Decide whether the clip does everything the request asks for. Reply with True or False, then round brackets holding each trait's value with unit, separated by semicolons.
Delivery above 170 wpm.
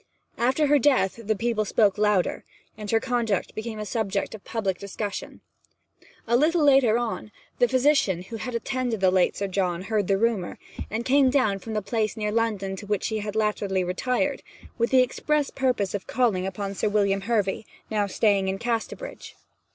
True (180 wpm)